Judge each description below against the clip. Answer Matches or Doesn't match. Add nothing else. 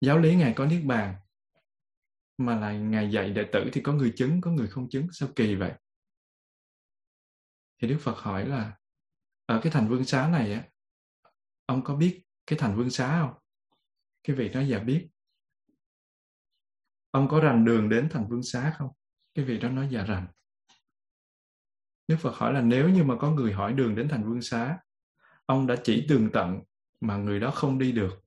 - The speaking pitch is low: Matches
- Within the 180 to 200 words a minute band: Matches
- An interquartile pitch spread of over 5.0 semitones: Matches